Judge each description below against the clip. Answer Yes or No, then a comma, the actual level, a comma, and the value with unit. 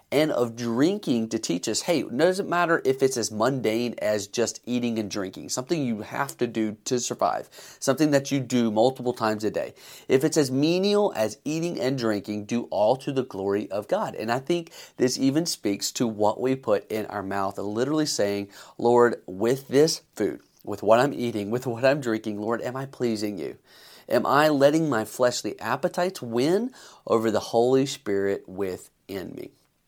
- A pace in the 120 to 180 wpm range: No, average, 190 wpm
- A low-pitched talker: Yes, low, 120 Hz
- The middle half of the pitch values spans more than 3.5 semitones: Yes, average, 4.1 semitones